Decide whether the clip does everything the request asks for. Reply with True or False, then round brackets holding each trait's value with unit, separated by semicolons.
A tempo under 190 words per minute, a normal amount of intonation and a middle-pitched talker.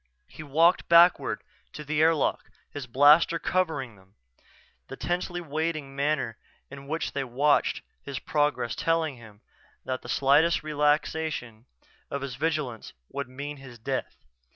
True (135 wpm; 3.5 semitones; 145 Hz)